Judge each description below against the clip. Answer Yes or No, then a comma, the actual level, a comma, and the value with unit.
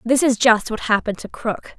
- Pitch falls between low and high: No, high, 230 Hz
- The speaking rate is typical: No, fast, 235 wpm